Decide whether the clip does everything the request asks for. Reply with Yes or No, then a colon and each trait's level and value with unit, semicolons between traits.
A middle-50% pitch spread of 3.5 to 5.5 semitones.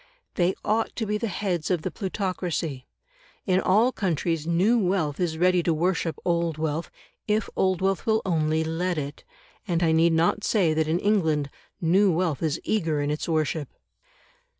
No: average, 3.1 semitones